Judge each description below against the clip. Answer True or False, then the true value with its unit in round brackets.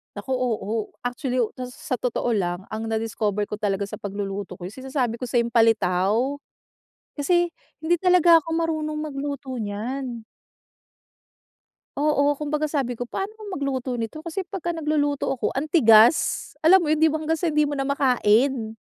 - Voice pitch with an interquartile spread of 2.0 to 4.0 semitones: False (5.4 semitones)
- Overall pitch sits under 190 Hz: False (265 Hz)